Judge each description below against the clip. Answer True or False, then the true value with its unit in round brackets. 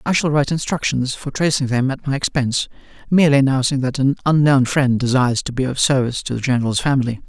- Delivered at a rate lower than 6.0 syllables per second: False (6.7 syllables/s)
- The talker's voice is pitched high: False (135 Hz)